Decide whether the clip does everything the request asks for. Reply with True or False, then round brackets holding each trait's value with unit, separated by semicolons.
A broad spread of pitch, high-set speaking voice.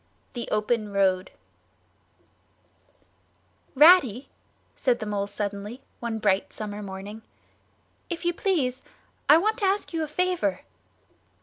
True (8.1 semitones; 235 Hz)